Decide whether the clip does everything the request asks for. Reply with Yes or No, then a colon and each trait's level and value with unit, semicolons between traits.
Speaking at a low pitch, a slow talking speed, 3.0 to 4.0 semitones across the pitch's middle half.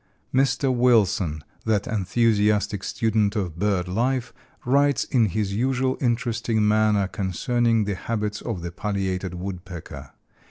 Yes: low, 105 Hz; slow, 125 wpm; average, 3.6 semitones